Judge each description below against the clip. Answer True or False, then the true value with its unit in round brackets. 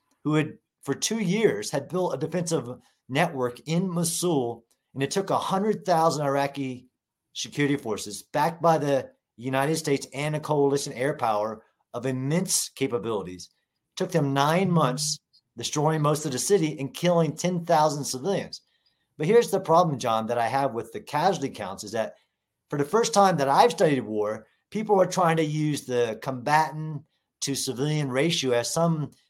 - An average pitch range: True (4.1 semitones)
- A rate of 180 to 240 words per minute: False (165 wpm)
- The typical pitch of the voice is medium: True (145 Hz)